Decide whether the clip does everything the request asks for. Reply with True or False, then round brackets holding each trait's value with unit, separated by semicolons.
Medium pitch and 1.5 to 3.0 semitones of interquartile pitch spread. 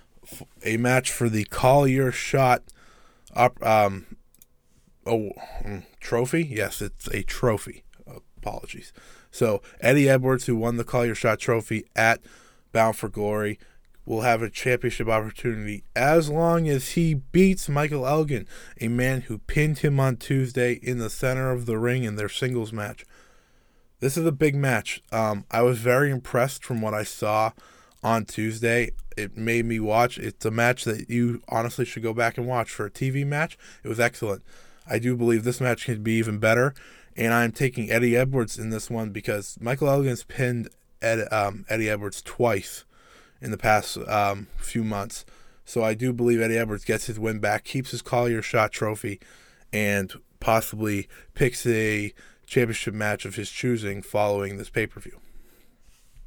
False (115 Hz; 2.7 semitones)